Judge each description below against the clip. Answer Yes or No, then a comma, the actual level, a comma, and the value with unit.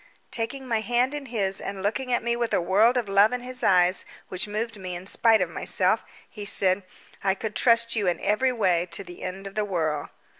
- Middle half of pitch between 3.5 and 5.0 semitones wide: Yes, average, 3.9 semitones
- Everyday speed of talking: No, fast, 225 wpm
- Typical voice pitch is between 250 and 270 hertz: No, high, 210 Hz